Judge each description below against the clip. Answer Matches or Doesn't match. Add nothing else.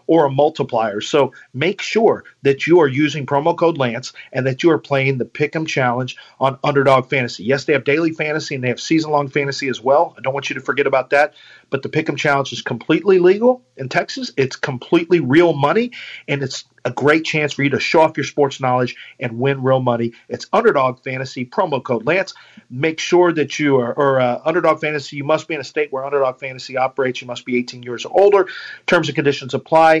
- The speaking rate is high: Matches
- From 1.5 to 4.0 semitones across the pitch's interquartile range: Matches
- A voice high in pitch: Doesn't match